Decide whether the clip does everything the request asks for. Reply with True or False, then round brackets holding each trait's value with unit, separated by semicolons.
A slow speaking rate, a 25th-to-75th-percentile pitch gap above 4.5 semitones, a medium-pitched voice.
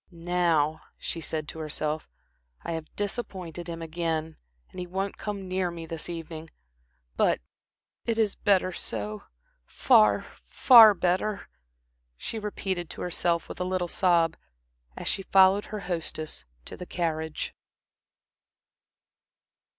False (125 wpm; 2.8 semitones; 175 Hz)